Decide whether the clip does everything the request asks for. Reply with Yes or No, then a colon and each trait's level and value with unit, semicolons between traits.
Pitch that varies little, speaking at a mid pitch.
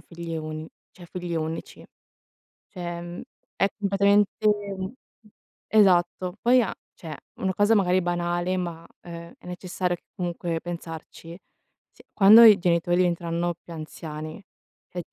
Yes: narrow, 2.1 semitones; medium, 175 Hz